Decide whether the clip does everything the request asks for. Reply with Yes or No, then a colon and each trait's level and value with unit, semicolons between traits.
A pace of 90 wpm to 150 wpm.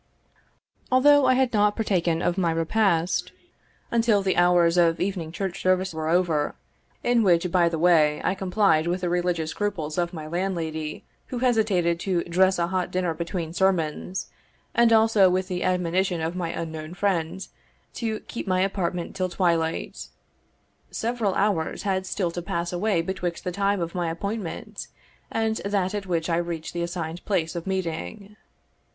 No: average, 165 wpm